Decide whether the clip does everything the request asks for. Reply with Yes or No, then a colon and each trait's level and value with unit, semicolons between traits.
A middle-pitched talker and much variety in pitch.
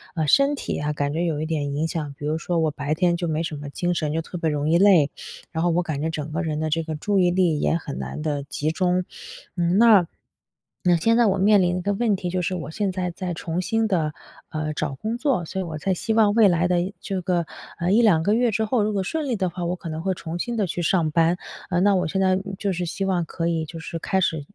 No: medium, 175 Hz; average, 3.3 semitones